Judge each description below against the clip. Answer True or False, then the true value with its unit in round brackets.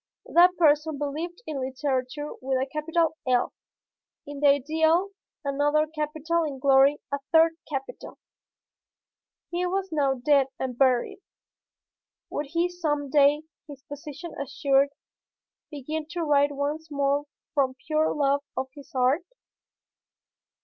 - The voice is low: False (290 Hz)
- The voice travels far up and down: False (2.4 semitones)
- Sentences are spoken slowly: True (125 wpm)